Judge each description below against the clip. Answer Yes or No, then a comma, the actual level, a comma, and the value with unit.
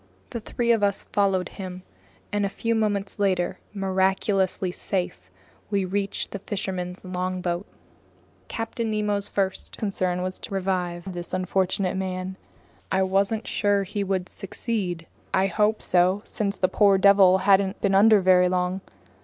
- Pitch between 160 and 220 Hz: Yes, high, 190 Hz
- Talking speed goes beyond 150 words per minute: No, average, 145 wpm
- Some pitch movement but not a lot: No, narrow, 1.7 semitones